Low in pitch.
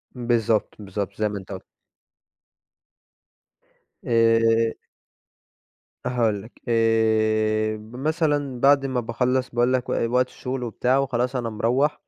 Yes: low, 120 Hz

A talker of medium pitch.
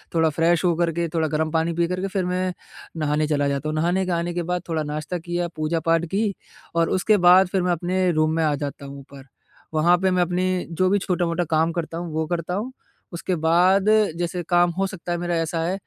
Yes: medium, 170 Hz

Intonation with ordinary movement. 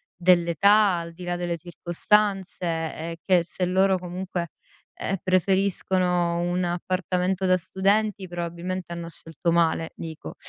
No: narrow, 1.7 semitones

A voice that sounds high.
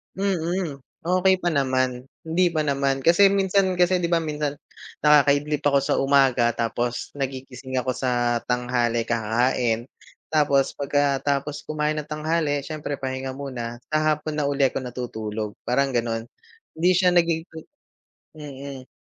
No: medium, 140 Hz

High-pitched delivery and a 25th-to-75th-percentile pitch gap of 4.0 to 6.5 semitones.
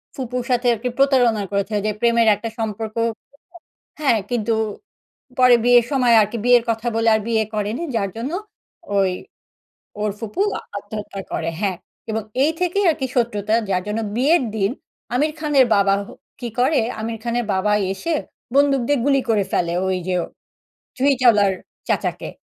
No: high, 230 Hz; average, 3.6 semitones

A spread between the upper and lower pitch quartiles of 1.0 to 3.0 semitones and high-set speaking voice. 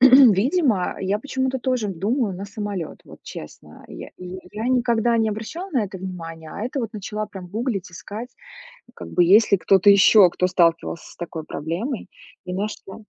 No: average, 4.6 semitones; high, 205 Hz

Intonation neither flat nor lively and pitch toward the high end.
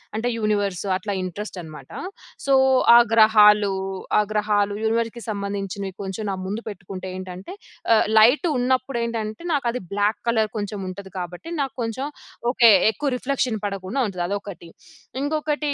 Yes: average, 3.2 semitones; high, 210 Hz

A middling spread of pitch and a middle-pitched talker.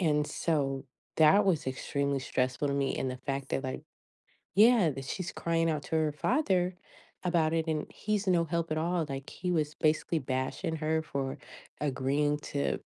Yes: average, 3.4 semitones; medium, 155 Hz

